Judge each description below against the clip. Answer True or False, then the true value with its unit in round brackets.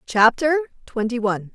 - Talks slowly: True (115 wpm)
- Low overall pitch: False (245 Hz)